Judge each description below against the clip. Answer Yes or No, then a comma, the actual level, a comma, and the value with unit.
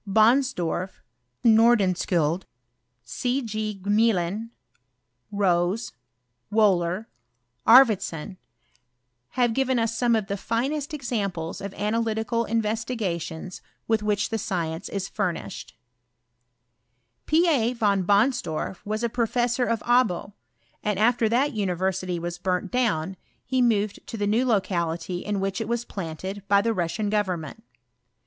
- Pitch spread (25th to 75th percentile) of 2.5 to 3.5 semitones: No, average, 4.1 semitones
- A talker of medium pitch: No, high, 210 Hz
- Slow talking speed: Yes, slow, 120 wpm